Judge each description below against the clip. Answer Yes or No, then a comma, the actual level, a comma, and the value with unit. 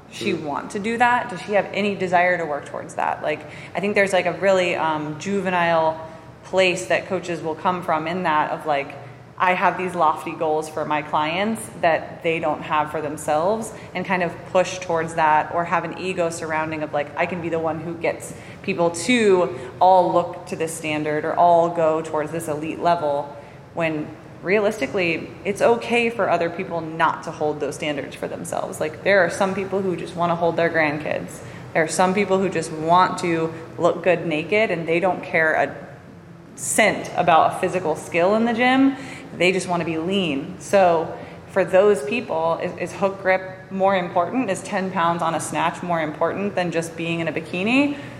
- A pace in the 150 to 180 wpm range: No, average, 200 wpm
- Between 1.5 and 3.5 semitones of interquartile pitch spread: Yes, average, 2.8 semitones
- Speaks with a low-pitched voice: No, medium, 170 Hz